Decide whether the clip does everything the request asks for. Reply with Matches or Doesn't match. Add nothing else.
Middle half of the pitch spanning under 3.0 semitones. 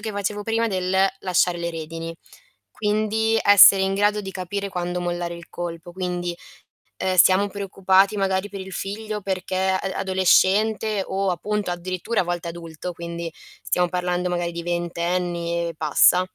Matches